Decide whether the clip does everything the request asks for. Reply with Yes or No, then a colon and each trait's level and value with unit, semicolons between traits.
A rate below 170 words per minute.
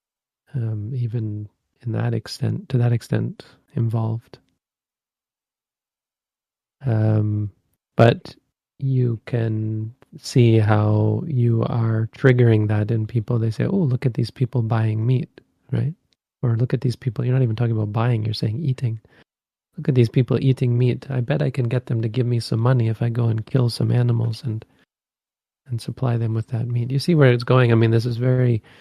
No: average, 180 wpm